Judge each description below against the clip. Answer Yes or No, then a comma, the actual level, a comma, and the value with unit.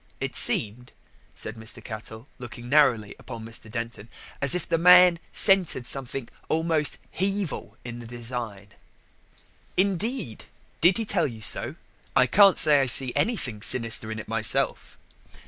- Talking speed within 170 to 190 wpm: No, average, 145 wpm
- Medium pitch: No, low, 125 Hz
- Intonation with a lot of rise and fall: Yes, wide, 7.1 semitones